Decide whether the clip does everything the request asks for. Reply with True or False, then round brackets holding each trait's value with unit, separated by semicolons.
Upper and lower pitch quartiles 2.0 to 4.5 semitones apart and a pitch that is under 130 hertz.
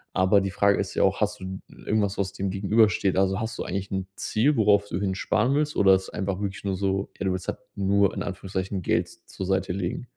False (1.2 semitones; 95 Hz)